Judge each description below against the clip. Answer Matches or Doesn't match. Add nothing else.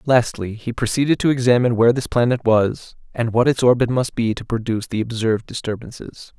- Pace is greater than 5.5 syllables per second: Matches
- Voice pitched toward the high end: Doesn't match